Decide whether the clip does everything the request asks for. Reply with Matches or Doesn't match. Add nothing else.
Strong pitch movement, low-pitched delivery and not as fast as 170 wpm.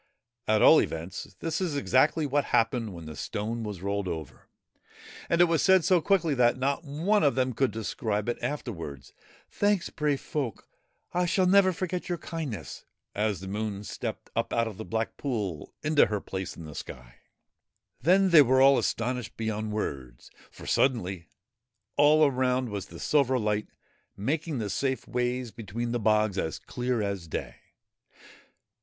Doesn't match